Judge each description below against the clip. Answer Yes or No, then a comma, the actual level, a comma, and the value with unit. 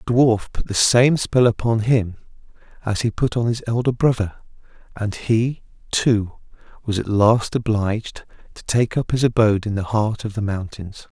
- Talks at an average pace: Yes, average, 180 wpm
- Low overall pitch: Yes, low, 110 Hz